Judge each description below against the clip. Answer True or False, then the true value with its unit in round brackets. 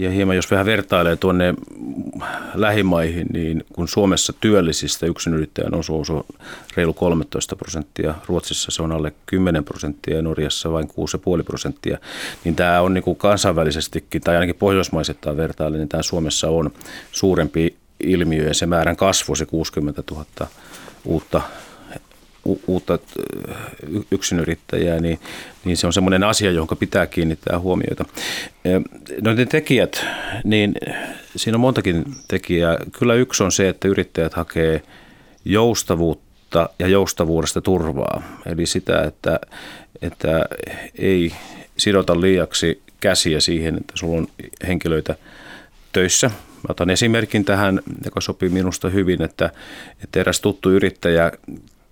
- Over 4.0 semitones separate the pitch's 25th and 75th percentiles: False (3.0 semitones)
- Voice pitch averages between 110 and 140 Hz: False (85 Hz)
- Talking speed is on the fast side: False (130 wpm)